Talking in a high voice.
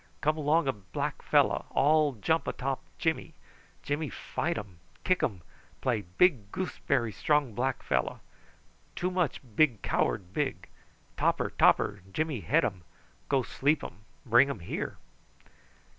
No: low, 135 Hz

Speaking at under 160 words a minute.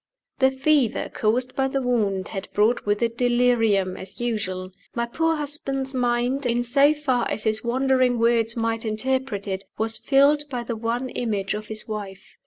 No: average, 175 wpm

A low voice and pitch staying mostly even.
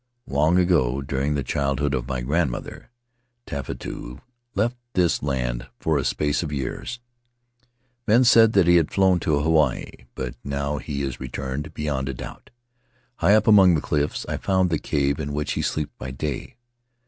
No: very low, 75 Hz; average, 4.3 semitones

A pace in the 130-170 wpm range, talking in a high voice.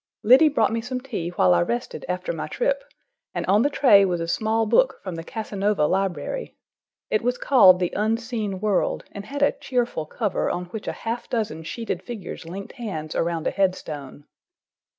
No: average, 185 wpm; high, 205 Hz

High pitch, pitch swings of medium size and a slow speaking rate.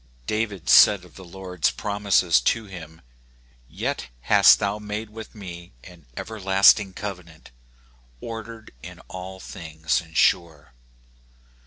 No: very low, 95 Hz; average, 3.9 semitones; slow, 125 wpm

